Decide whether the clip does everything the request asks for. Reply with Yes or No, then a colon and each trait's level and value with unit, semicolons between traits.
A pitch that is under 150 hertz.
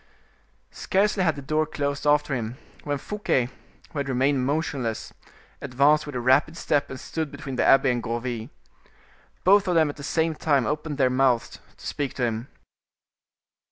Yes: medium, 140 Hz